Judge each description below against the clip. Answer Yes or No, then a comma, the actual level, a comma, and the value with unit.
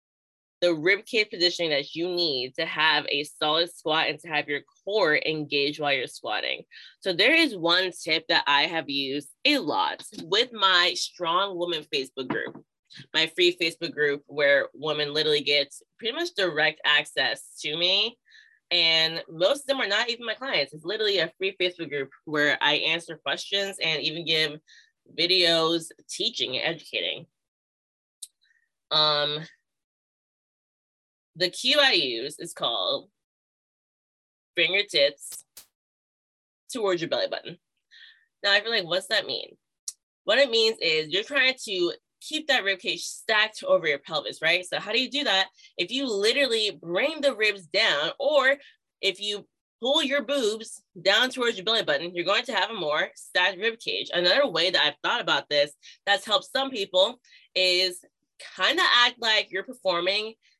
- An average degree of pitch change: No, wide, 9.0 semitones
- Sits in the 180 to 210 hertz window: Yes, high, 190 Hz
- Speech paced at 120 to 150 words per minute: No, average, 160 wpm